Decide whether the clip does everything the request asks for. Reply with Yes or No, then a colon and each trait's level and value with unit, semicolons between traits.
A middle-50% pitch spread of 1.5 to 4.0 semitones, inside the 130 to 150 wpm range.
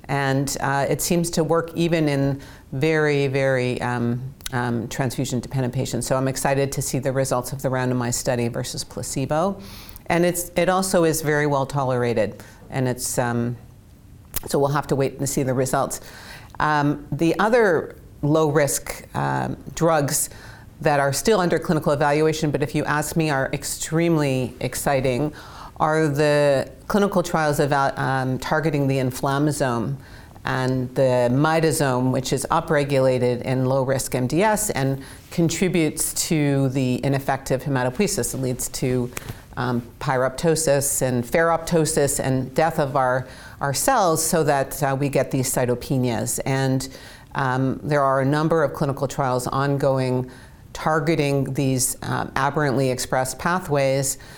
Yes: average, 3.0 semitones; average, 140 wpm